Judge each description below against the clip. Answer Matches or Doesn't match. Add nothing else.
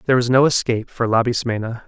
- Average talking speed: Matches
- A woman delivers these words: Doesn't match